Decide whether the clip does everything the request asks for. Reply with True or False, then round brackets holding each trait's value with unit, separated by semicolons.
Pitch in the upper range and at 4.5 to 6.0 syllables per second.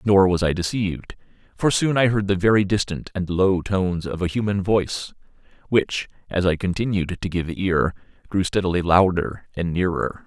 False (95 Hz; 5.0 syllables/s)